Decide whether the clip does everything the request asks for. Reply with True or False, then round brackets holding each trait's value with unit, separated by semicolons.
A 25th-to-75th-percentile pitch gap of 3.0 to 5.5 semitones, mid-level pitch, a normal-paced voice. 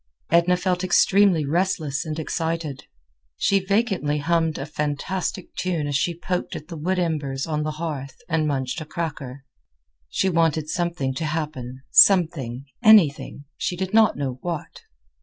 True (3.7 semitones; 160 Hz; 145 wpm)